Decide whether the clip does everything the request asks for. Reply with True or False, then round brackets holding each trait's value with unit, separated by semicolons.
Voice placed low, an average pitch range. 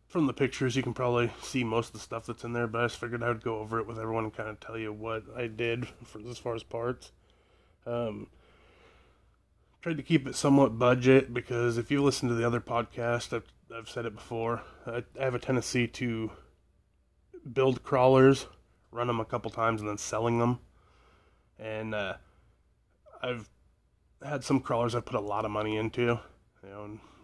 False (120 Hz; 1.9 semitones)